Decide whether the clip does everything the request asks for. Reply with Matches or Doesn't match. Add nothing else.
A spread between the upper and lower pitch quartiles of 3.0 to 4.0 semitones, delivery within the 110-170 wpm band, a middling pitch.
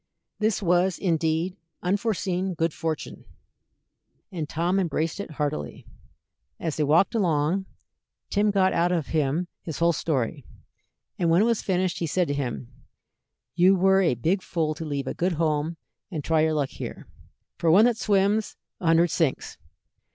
Matches